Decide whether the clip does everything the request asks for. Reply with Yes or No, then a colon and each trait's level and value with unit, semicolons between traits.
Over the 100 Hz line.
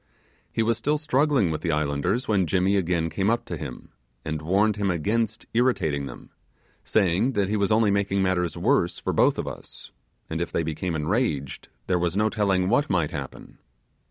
No: very low, 95 Hz